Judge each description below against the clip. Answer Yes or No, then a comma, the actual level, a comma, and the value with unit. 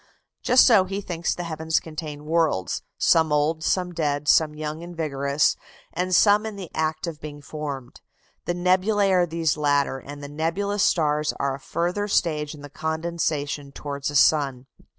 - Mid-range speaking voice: Yes, medium, 160 Hz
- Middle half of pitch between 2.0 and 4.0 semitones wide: Yes, average, 3.1 semitones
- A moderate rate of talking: Yes, average, 170 wpm